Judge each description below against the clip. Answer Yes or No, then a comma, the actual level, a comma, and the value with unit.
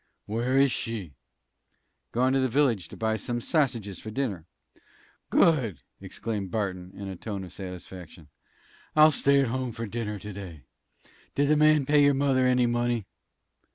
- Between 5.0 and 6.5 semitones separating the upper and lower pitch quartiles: Yes, average, 5.3 semitones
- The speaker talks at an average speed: Yes, average, 160 wpm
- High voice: No, low, 115 Hz